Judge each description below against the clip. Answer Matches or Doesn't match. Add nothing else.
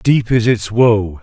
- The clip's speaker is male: Matches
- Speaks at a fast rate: Doesn't match